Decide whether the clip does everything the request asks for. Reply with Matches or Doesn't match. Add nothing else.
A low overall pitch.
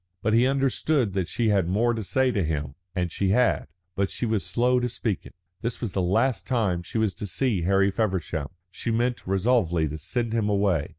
Matches